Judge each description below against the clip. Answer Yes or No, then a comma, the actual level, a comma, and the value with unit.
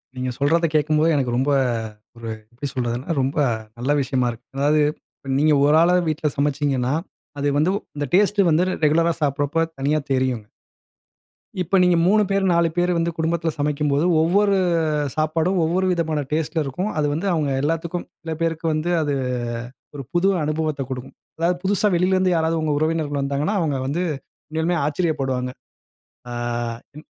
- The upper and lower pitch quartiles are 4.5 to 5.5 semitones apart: No, average, 3.1 semitones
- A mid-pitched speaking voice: Yes, medium, 155 Hz